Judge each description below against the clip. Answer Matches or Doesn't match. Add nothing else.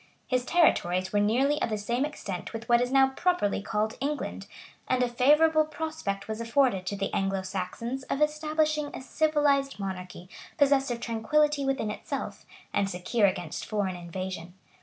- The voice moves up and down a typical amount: Doesn't match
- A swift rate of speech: Doesn't match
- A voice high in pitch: Matches